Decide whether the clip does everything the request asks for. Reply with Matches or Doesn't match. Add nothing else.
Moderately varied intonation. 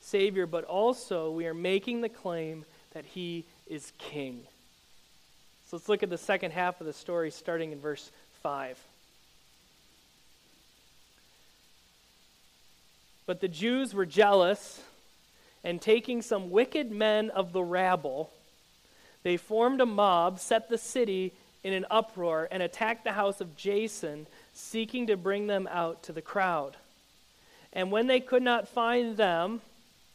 Matches